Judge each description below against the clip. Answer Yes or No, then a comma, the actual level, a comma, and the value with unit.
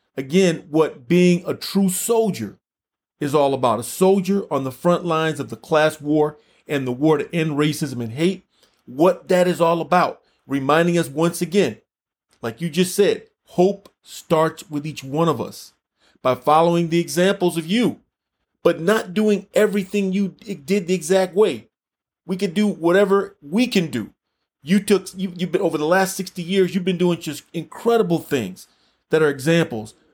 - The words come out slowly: No, average, 175 wpm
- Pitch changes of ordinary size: Yes, average, 3.9 semitones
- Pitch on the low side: No, medium, 175 Hz